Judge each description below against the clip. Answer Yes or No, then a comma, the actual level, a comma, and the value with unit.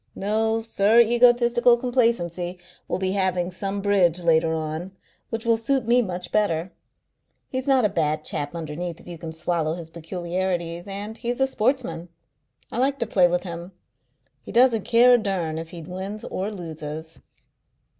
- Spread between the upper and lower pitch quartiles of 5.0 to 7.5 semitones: Yes, average, 5.3 semitones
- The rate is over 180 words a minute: No, average, 165 wpm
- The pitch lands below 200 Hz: Yes, high, 190 Hz